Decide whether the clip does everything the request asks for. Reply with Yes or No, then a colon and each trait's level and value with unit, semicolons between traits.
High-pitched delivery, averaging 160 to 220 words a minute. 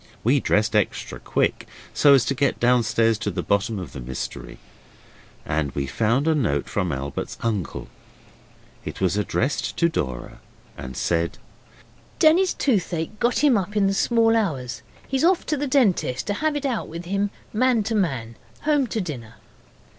No: medium, 140 Hz; average, 170 wpm